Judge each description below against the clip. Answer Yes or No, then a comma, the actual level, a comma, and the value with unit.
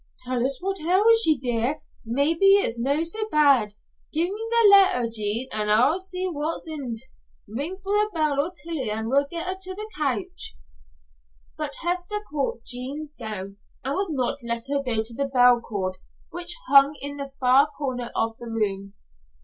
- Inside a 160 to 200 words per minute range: Yes, average, 175 wpm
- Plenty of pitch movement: Yes, wide, 6.7 semitones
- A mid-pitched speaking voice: No, very high, 280 Hz